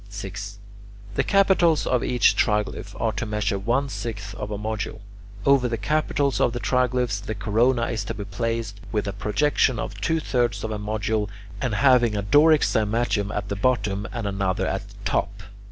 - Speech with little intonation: No, average, 3.5 semitones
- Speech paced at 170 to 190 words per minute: Yes, average, 185 wpm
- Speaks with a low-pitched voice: Yes, low, 110 Hz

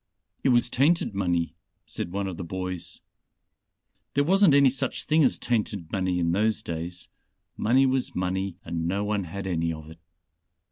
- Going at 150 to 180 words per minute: Yes, average, 170 wpm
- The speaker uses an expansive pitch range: Yes, wide, 6.1 semitones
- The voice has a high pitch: No, very low, 95 Hz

